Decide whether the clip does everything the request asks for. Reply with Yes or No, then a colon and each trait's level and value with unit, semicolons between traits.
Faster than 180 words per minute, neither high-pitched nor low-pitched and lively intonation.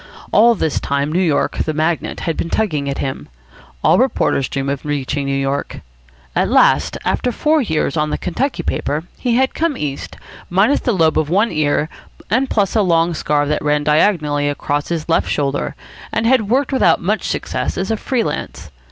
Yes: average, 190 wpm; medium, 160 Hz; wide, 7.0 semitones